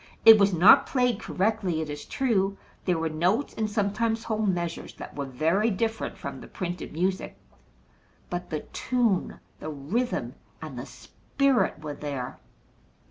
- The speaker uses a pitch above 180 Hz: Yes, high, 190 Hz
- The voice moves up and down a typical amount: No, wide, 5.7 semitones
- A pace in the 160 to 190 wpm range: No, average, 150 wpm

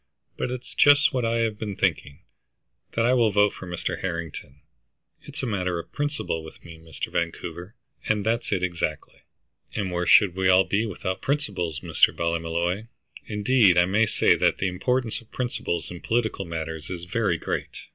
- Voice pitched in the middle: No, very low, 95 Hz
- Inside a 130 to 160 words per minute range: No, average, 175 wpm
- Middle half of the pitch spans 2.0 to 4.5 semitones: No, average, 5.0 semitones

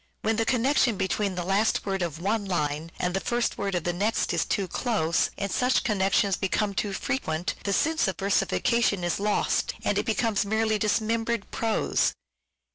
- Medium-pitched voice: No, high, 200 Hz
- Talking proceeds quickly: No, average, 185 wpm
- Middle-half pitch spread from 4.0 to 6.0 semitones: No, average, 3.2 semitones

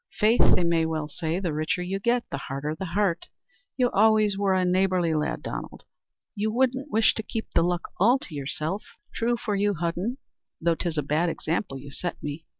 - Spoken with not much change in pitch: No, average, 4.8 semitones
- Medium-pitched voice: Yes, medium, 180 Hz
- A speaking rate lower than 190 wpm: No, average, 200 wpm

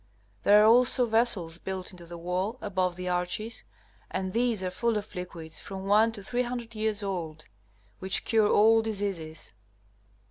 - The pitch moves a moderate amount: Yes, average, 3.7 semitones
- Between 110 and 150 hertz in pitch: No, high, 200 Hz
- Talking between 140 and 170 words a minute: Yes, average, 155 wpm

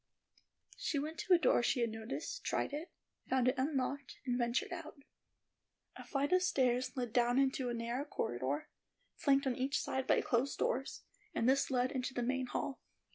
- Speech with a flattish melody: Yes, narrow, 2.3 semitones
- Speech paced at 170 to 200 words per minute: Yes, average, 185 wpm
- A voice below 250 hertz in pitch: No, very high, 260 Hz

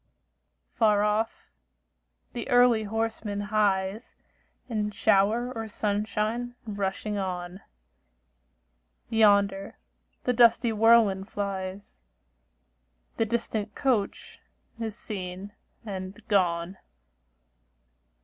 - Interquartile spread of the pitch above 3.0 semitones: No, narrow, 2.4 semitones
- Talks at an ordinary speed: No, slow, 80 wpm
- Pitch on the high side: Yes, high, 210 Hz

